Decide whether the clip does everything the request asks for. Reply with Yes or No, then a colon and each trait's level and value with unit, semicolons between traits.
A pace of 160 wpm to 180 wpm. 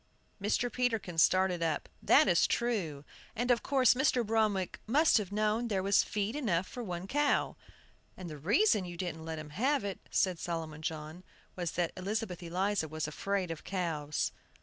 Yes: average, 170 wpm